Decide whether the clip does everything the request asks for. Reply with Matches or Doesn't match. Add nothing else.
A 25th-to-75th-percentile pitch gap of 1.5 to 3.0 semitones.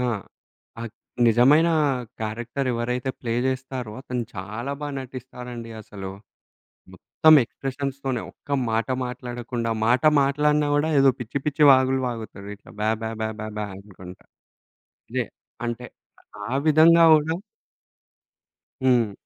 Doesn't match